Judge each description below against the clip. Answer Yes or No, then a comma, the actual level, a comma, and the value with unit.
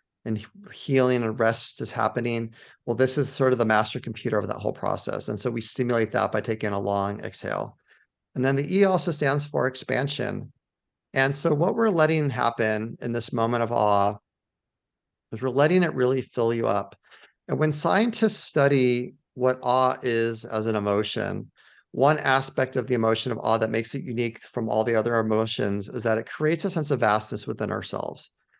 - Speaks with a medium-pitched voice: No, low, 120 Hz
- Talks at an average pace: Yes, average, 190 wpm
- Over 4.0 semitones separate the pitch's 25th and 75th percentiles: No, average, 3.4 semitones